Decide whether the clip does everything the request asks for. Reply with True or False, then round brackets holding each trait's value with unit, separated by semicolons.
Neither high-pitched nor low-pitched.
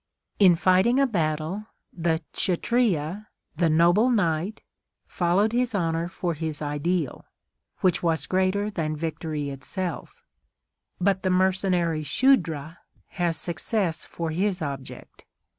True (175 Hz)